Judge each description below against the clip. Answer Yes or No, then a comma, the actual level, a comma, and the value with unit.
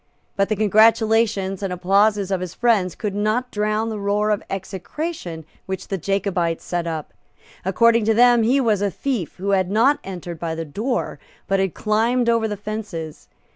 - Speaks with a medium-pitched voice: No, high, 205 Hz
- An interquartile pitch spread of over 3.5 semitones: No, average, 3.1 semitones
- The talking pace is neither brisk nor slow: Yes, average, 175 wpm